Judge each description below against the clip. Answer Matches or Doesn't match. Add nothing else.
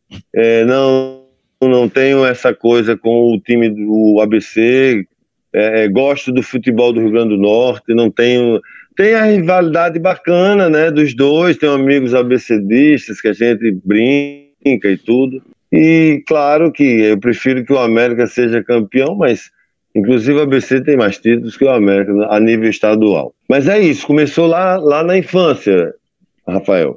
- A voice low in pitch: Matches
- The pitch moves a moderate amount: Matches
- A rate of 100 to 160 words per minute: Matches